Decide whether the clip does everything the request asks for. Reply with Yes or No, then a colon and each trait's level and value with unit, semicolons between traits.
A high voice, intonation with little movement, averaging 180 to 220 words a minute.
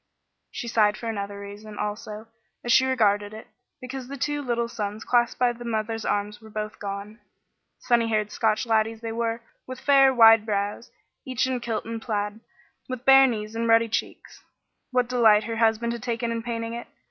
Yes: high, 225 Hz; narrow, 2.1 semitones; average, 185 wpm